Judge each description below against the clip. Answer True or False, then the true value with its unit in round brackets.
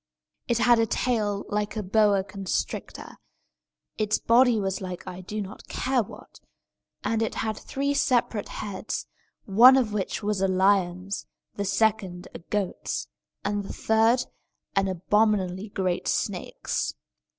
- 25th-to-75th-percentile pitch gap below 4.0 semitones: True (2.8 semitones)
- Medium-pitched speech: False (205 Hz)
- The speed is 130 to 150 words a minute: True (140 wpm)